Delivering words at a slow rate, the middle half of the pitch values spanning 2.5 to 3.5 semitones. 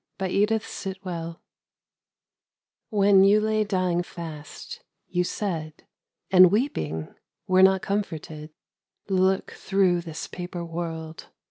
Yes: slow, 110 wpm; average, 3.0 semitones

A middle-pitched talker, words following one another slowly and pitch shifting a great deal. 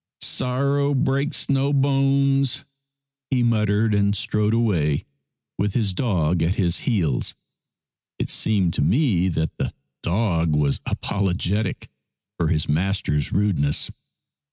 No: low, 105 Hz; slow, 115 wpm; wide, 7.1 semitones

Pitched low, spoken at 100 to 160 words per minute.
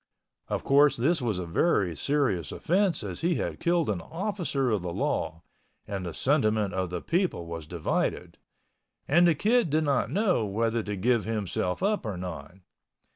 No: low, 115 Hz; average, 170 wpm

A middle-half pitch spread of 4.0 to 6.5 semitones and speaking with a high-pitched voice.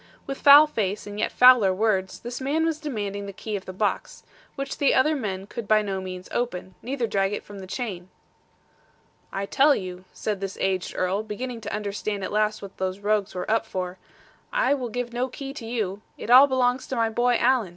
Yes: average, 4.5 semitones; high, 215 Hz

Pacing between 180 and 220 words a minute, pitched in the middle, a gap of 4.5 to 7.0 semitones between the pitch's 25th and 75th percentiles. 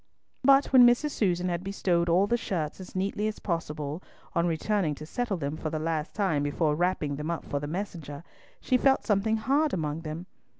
Yes: average, 200 wpm; medium, 175 Hz; average, 5.3 semitones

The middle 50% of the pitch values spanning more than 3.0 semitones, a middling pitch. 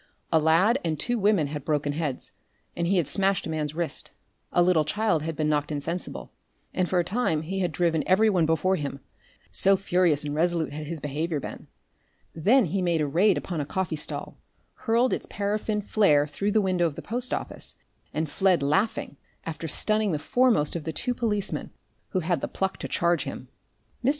Yes: average, 4.4 semitones; medium, 170 Hz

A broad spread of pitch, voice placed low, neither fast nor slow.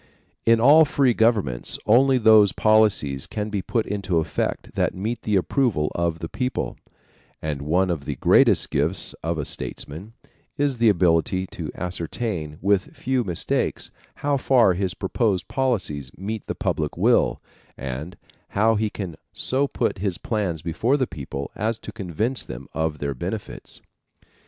Yes: wide, 5.7 semitones; low, 100 Hz; average, 155 wpm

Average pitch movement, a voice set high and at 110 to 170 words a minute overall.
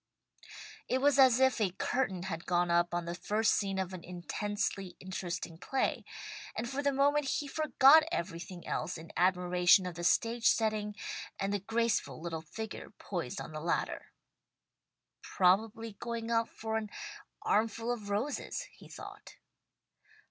Yes: average, 4.7 semitones; high, 205 Hz; average, 150 wpm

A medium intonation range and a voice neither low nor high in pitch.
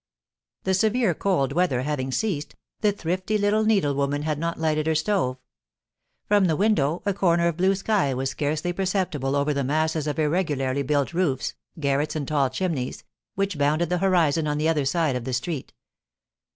Yes: average, 4.7 semitones; medium, 155 Hz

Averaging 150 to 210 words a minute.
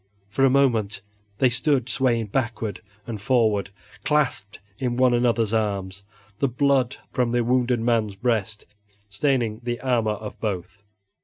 No: average, 140 wpm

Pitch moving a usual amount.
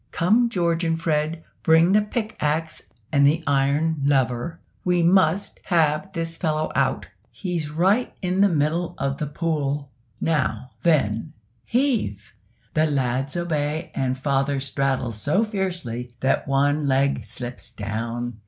Yes: average, 4.0 semitones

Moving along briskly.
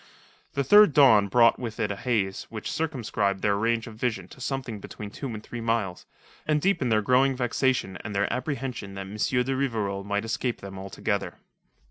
No: average, 185 wpm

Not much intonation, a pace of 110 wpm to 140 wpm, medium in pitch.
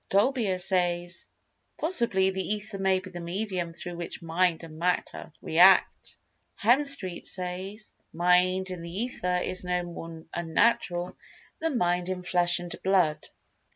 Yes: narrow, 1.8 semitones; slow, 135 wpm; medium, 180 Hz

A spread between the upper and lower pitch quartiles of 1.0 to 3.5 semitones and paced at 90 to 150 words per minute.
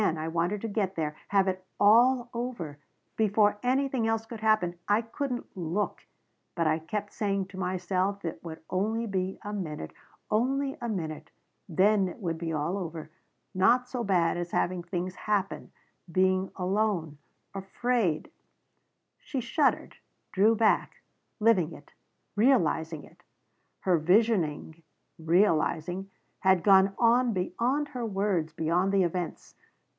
No: average, 4.4 semitones; average, 140 wpm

